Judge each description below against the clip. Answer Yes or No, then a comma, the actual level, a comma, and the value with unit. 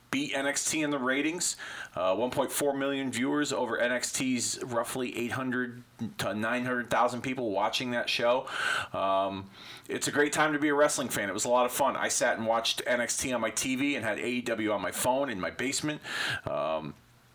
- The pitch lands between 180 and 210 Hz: No, low, 130 Hz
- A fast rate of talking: No, average, 185 wpm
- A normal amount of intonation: Yes, average, 3.6 semitones